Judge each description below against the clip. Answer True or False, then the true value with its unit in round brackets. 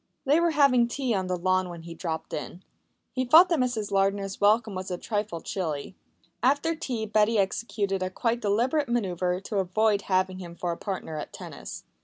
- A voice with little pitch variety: False (4.4 semitones)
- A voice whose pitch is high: True (200 Hz)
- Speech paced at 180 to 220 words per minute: True (190 wpm)